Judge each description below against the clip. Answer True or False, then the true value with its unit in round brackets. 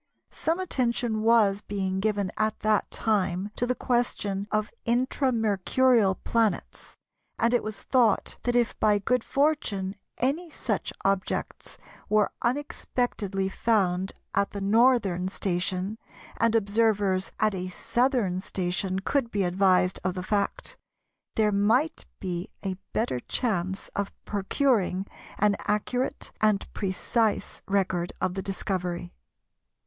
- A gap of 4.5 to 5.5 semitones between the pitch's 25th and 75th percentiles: False (3.6 semitones)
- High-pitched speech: True (205 Hz)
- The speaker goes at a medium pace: False (125 wpm)